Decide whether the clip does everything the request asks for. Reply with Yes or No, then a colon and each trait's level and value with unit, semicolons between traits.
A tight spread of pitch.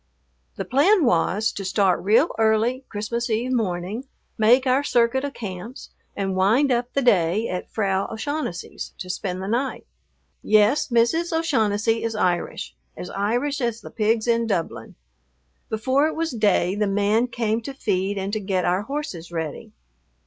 No: average, 4.4 semitones